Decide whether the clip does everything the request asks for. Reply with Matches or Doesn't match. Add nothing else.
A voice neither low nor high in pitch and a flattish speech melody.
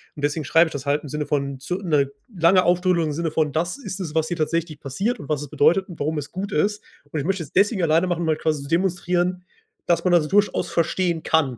Doesn't match